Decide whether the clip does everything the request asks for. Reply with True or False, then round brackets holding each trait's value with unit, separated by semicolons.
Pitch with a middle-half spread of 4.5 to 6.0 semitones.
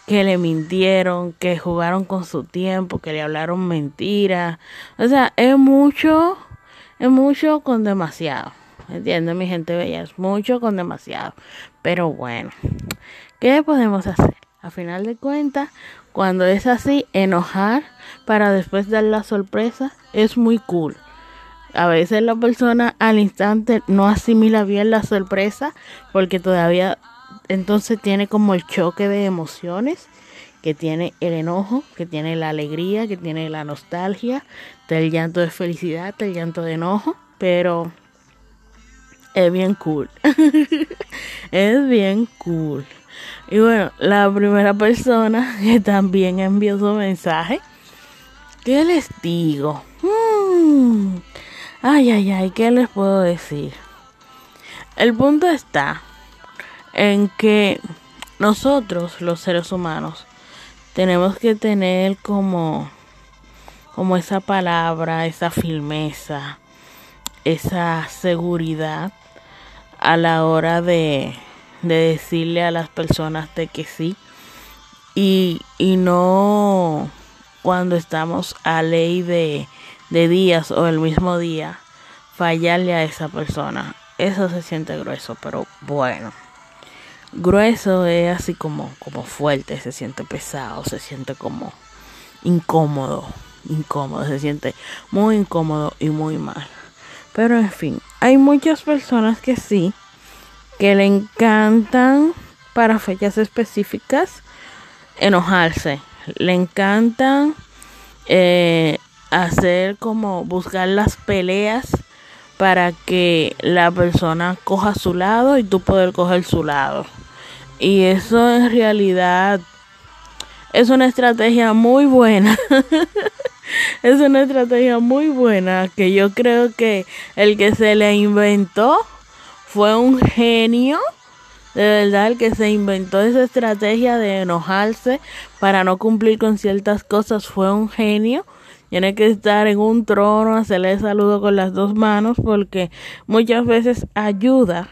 True (4.8 semitones)